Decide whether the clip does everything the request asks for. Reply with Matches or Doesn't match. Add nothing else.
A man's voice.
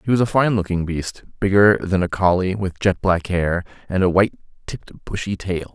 Matches